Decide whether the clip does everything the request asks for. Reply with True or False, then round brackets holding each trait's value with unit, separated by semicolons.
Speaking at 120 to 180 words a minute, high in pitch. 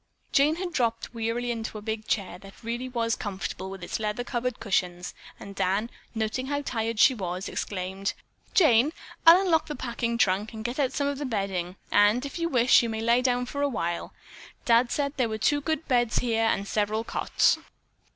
False (200 wpm; 230 Hz)